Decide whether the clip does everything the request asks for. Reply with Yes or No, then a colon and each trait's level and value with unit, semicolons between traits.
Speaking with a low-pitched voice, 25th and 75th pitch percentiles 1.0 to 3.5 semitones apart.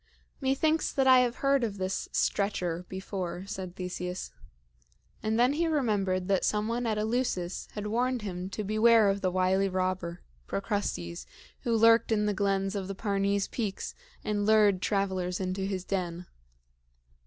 No: high, 200 Hz; average, 3.1 semitones